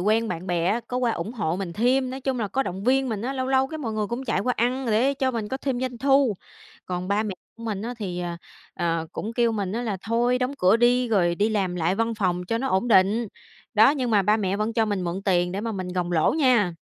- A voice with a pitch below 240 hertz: Yes, high, 220 Hz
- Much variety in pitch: No, average, 4.8 semitones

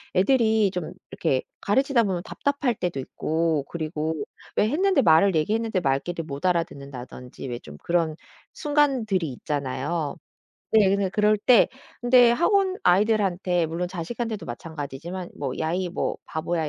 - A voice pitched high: No, medium, 180 Hz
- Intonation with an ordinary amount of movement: No, wide, 5.8 semitones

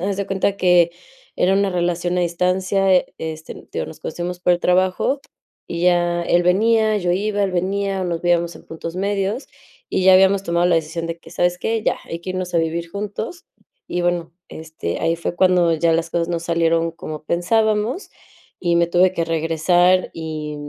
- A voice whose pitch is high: No, medium, 175 Hz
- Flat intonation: Yes, narrow, 2.2 semitones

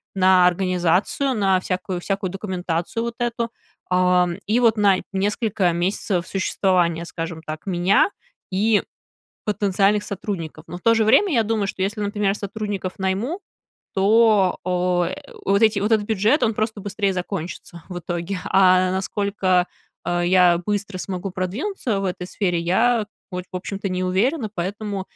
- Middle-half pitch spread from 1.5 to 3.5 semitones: Yes, narrow, 2.6 semitones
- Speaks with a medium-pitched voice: No, high, 195 Hz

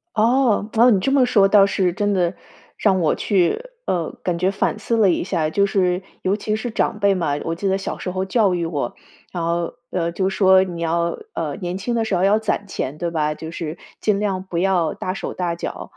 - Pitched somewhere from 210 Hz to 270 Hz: No, high, 190 Hz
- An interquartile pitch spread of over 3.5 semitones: No, average, 3.1 semitones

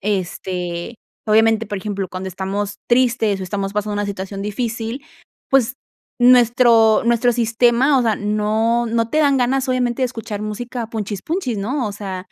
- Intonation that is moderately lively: Yes, average, 3.1 semitones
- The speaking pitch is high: Yes, high, 225 Hz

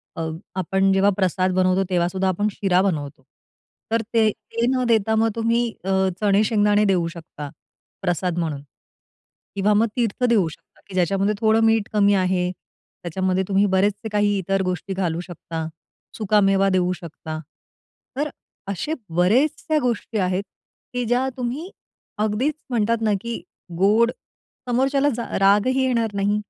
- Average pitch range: Yes, average, 3.6 semitones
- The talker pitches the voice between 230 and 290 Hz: No, high, 200 Hz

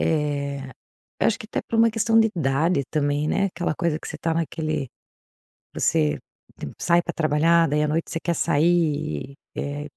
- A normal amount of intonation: Yes, average, 3.0 semitones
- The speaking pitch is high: No, medium, 155 Hz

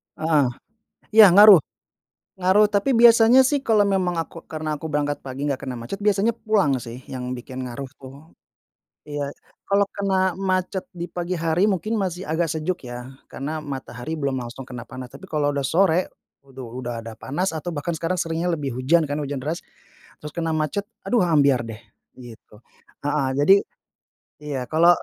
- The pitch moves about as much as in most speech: No, wide, 5.8 semitones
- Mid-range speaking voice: Yes, medium, 155 Hz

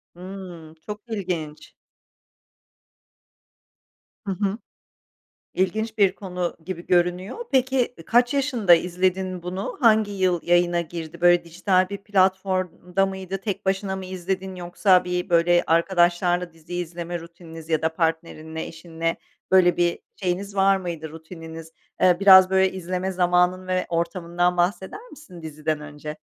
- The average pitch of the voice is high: No, medium, 180 Hz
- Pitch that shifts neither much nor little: No, narrow, 2.0 semitones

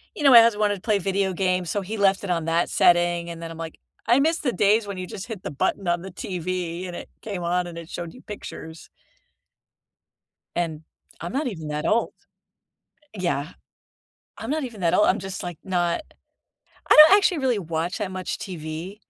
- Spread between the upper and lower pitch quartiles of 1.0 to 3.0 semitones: No, average, 3.5 semitones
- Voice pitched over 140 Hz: Yes, medium, 185 Hz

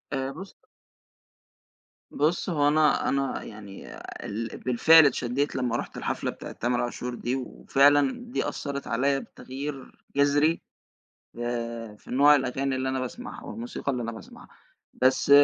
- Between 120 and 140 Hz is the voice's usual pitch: Yes, low, 135 Hz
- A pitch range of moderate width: Yes, average, 3.0 semitones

